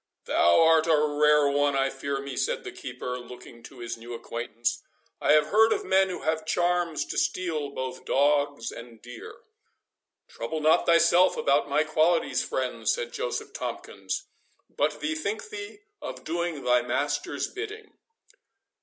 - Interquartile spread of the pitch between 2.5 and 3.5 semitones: No, average, 4.9 semitones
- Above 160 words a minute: No, average, 155 wpm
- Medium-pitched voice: Yes, medium, 150 Hz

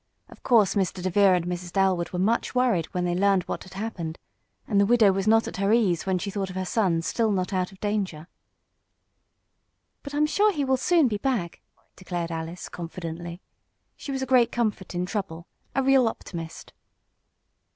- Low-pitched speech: No, high, 195 Hz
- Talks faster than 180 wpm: Yes, average, 190 wpm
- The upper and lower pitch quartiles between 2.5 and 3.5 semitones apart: No, average, 4.3 semitones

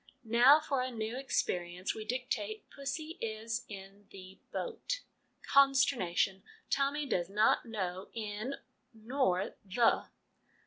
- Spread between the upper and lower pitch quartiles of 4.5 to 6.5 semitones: Yes, wide, 5.6 semitones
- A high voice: Yes, high, 225 Hz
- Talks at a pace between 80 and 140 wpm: Yes, slow, 135 wpm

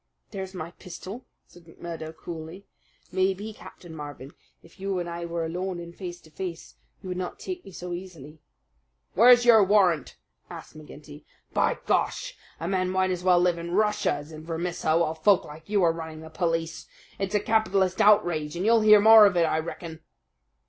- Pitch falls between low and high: Yes, medium, 175 Hz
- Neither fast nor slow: Yes, average, 185 wpm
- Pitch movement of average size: Yes, average, 3.1 semitones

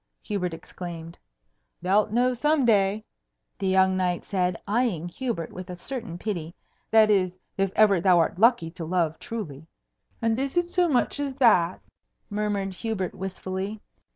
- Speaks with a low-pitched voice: No, high, 195 Hz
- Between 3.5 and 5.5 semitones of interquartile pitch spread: Yes, average, 4.1 semitones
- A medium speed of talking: Yes, average, 155 wpm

